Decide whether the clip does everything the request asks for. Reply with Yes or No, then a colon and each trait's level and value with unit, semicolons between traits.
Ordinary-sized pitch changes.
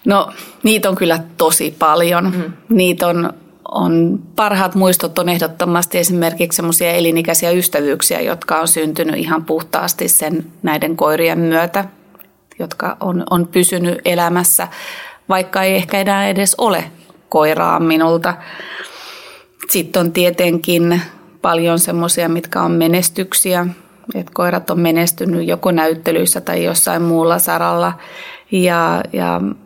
No: narrow, 1.6 semitones